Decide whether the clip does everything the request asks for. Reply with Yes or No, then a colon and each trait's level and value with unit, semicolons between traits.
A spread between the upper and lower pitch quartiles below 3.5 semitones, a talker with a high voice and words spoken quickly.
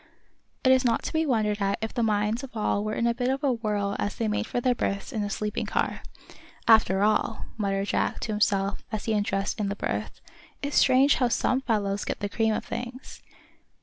Yes: average, 3.1 semitones; high, 220 Hz; fast, 220 wpm